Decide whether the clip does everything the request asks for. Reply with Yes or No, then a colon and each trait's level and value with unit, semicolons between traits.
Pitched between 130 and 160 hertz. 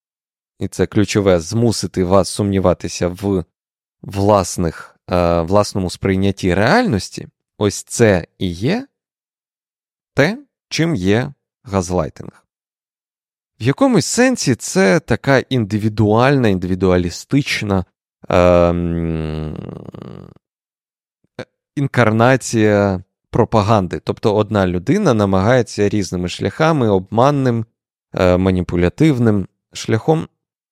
No: low, 105 Hz